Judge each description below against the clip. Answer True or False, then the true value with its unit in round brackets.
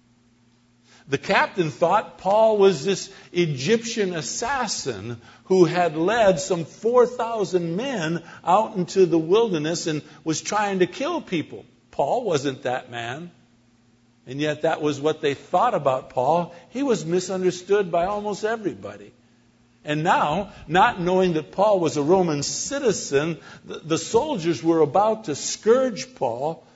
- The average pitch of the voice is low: False (170 Hz)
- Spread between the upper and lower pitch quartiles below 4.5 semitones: False (5.2 semitones)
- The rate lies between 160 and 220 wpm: False (135 wpm)